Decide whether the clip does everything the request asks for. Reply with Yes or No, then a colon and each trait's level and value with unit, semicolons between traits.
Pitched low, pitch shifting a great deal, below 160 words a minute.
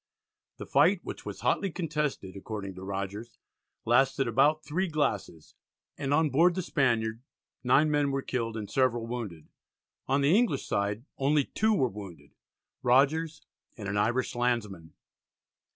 Yes: low, 125 Hz; wide, 5.8 semitones; average, 145 wpm